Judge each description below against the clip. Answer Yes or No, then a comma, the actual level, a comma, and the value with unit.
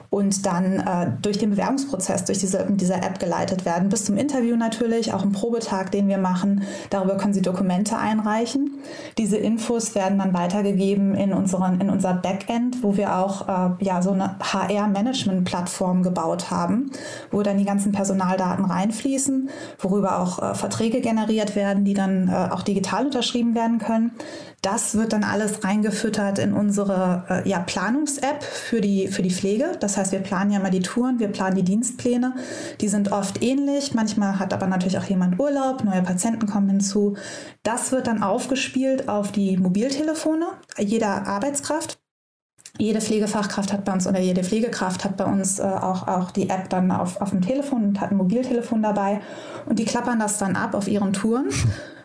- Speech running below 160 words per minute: No, average, 180 wpm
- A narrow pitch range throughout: No, average, 3.4 semitones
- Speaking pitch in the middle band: No, high, 205 Hz